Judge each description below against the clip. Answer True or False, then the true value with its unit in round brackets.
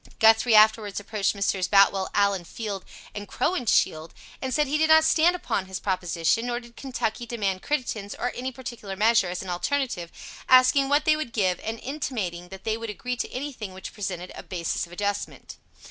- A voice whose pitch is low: False (215 Hz)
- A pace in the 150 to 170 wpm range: False (185 wpm)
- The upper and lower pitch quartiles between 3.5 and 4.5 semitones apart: False (5.0 semitones)